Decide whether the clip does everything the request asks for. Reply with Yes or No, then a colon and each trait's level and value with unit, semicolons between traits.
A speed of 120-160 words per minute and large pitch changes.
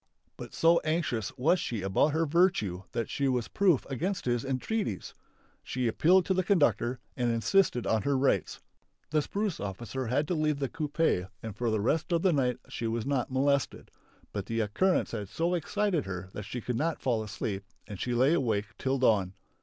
No: average, 195 wpm; wide, 6.5 semitones